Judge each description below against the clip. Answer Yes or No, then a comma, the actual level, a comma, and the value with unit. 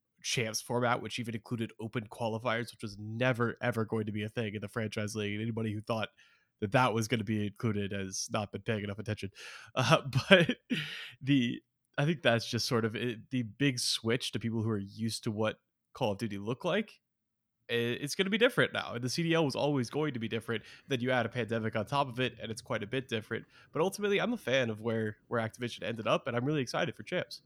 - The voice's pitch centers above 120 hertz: No, low, 115 Hz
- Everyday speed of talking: No, fast, 240 wpm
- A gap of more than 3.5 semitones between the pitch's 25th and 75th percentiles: No, narrow, 2.5 semitones